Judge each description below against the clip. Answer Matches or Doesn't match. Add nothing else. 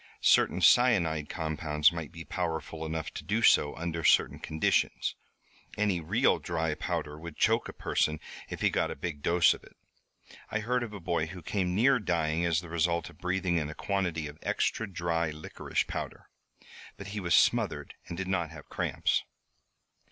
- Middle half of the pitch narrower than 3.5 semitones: Matches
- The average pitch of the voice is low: Matches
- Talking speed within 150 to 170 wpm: Doesn't match